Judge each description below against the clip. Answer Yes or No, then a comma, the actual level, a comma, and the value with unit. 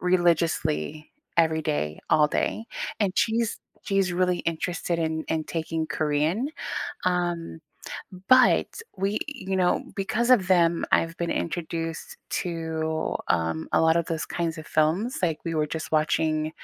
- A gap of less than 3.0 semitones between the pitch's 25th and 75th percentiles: Yes, narrow, 2.5 semitones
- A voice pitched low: No, medium, 165 Hz